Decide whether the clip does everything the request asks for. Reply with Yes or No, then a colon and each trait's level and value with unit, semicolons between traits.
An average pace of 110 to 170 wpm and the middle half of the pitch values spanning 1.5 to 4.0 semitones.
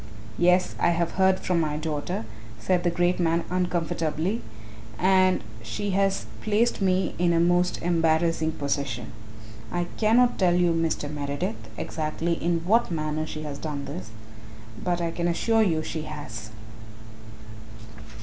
Yes: average, 145 wpm; average, 2.9 semitones